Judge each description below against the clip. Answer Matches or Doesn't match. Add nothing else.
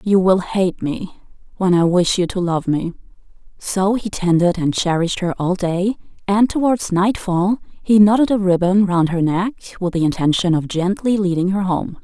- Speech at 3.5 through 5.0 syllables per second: Matches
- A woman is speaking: Matches